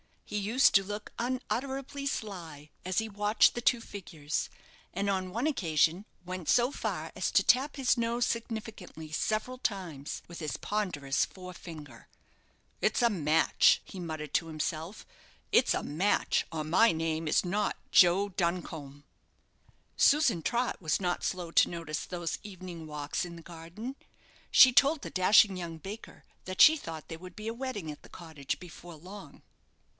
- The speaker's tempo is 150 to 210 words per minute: Yes, average, 160 wpm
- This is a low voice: No, medium, 185 Hz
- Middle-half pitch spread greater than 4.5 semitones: Yes, wide, 5.4 semitones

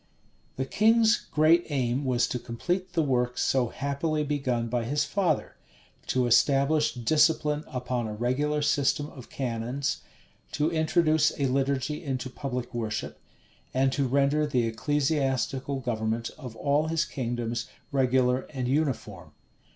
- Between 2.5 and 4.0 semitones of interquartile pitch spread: Yes, average, 3.4 semitones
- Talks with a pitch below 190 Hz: Yes, low, 135 Hz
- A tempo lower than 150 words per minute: Yes, slow, 135 wpm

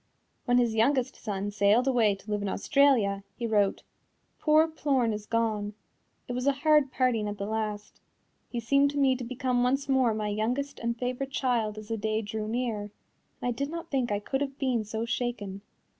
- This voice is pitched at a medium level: No, high, 235 Hz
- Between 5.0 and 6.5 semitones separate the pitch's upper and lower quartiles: No, average, 3.9 semitones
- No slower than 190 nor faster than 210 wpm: Yes, average, 200 wpm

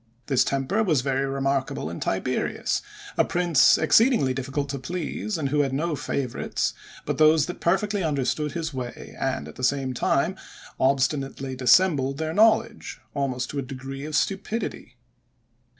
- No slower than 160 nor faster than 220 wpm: No, average, 150 wpm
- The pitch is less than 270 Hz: Yes, medium, 140 Hz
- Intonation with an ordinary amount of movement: Yes, average, 3.9 semitones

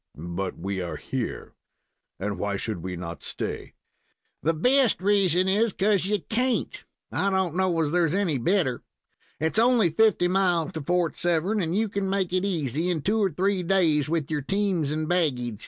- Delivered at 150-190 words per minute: Yes, average, 180 wpm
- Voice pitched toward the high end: No, medium, 175 Hz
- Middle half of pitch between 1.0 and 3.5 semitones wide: No, average, 4.8 semitones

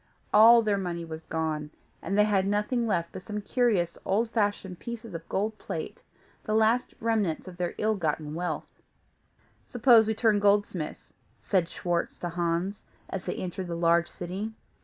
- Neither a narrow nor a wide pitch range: Yes, average, 4.1 semitones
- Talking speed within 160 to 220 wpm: Yes, average, 165 wpm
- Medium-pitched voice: No, high, 195 Hz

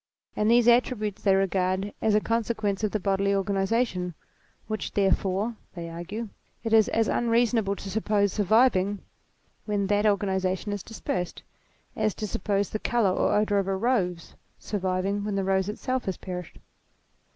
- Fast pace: No, average, 155 wpm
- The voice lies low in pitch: No, high, 205 Hz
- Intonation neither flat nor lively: No, narrow, 2.3 semitones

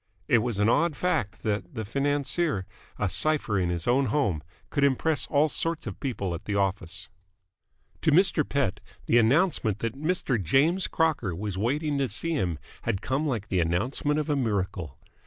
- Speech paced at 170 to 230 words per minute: Yes, average, 175 wpm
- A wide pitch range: Yes, wide, 7.1 semitones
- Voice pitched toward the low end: Yes, low, 125 Hz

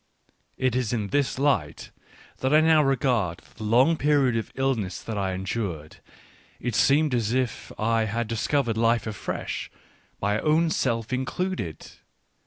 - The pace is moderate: Yes, average, 145 wpm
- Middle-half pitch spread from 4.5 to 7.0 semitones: No, average, 4.1 semitones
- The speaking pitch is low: Yes, low, 120 Hz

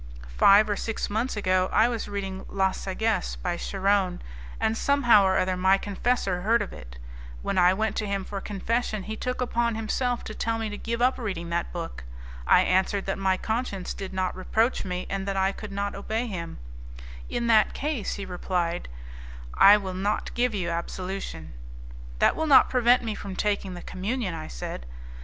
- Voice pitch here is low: No, high, 200 Hz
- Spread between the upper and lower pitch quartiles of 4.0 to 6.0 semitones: No, average, 3.2 semitones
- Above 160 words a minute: Yes, average, 190 wpm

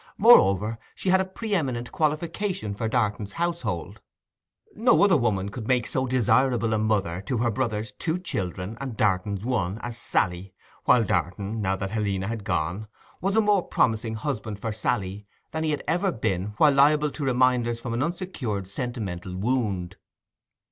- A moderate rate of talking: Yes, average, 160 wpm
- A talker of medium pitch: No, low, 115 Hz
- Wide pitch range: Yes, wide, 5.9 semitones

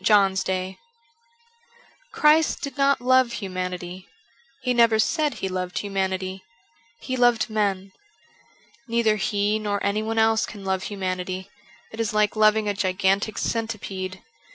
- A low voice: No, high, 205 Hz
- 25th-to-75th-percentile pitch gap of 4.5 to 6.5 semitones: No, average, 3.0 semitones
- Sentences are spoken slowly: Yes, slow, 130 wpm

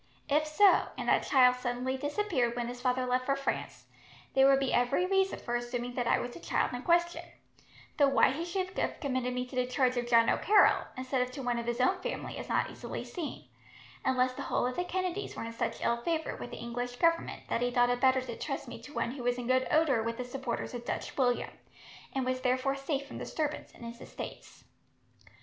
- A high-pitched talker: Yes, very high, 255 Hz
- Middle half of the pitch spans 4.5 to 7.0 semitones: No, average, 2.9 semitones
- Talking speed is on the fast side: Yes, fast, 230 wpm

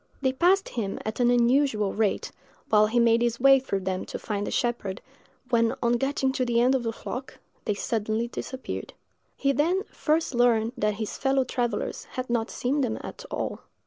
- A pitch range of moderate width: Yes, average, 3.3 semitones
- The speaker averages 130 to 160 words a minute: No, average, 190 wpm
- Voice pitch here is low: No, high, 240 Hz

